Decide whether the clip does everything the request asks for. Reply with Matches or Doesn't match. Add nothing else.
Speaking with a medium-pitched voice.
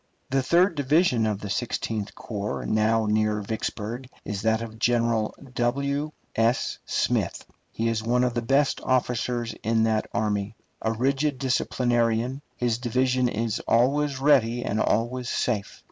Doesn't match